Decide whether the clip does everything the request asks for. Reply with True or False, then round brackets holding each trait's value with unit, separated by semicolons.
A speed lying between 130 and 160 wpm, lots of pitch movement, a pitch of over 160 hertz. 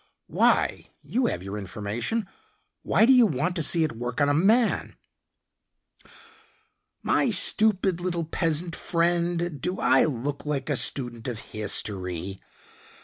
False (135 wpm; 6.9 semitones; 150 Hz)